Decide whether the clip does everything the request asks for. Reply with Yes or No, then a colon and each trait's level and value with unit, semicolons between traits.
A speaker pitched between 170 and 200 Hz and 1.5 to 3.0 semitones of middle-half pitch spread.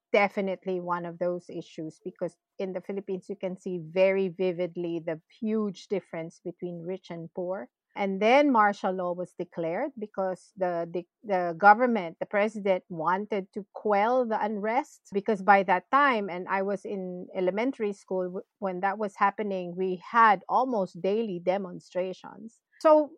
Yes: high, 190 Hz; average, 2.7 semitones